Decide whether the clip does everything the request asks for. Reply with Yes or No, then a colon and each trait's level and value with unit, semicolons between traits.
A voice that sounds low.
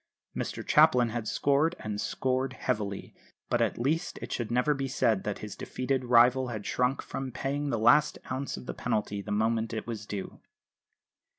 Yes: low, 120 Hz